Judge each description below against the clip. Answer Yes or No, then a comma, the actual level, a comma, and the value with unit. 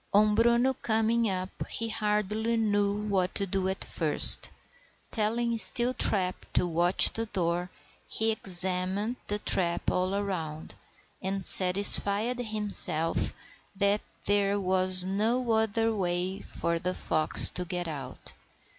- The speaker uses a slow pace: Yes, slow, 125 wpm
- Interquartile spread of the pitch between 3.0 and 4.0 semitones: Yes, average, 3.3 semitones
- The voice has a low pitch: No, high, 200 Hz